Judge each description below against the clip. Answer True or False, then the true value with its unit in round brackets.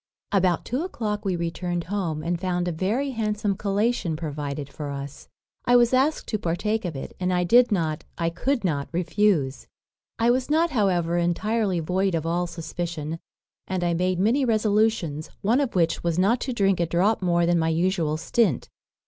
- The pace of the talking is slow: False (180 wpm)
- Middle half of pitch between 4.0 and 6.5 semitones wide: True (4.4 semitones)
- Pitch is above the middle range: False (180 Hz)